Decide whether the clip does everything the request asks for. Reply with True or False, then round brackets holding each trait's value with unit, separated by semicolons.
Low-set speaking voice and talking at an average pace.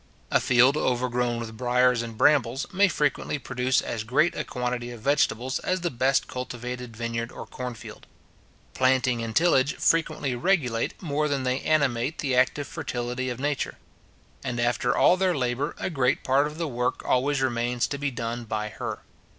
True (125 Hz; 175 wpm)